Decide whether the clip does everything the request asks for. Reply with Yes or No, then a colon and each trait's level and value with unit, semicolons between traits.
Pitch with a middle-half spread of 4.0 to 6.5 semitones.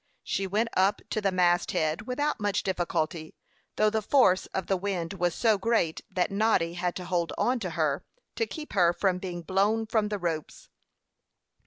No: average, 3.5 semitones